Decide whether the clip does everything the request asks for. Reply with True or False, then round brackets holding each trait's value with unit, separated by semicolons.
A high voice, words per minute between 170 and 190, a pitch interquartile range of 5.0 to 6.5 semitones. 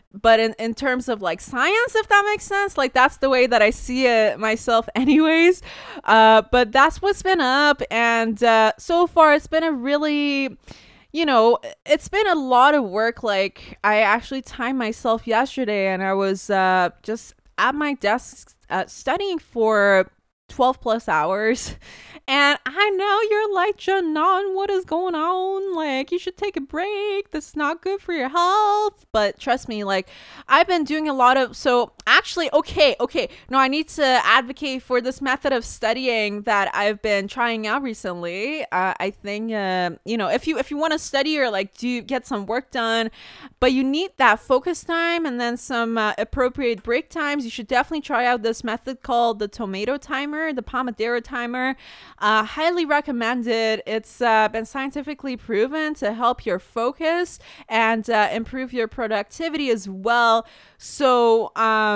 True (250 Hz; 180 wpm; 5.3 semitones)